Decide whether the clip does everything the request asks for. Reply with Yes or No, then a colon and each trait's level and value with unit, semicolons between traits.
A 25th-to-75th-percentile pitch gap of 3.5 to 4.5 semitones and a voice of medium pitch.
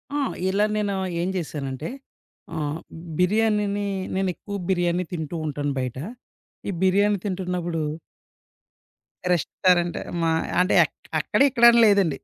Yes: average, 3.8 semitones; medium, 180 Hz